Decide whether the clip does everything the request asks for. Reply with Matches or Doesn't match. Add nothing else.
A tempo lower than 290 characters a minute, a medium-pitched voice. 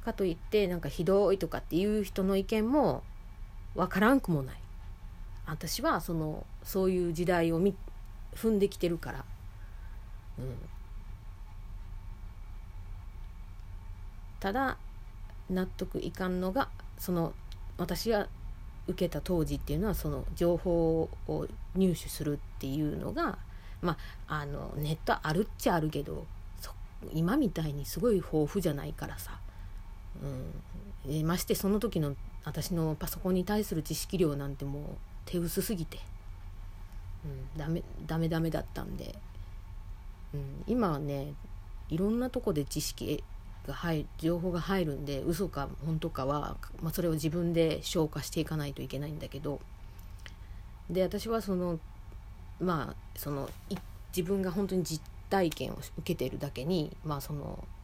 Matches